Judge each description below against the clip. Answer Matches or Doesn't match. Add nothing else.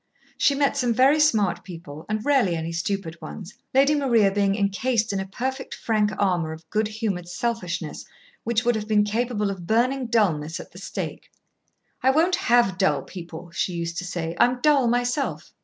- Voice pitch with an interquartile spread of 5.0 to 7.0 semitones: Matches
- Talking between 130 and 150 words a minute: Doesn't match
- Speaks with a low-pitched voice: Doesn't match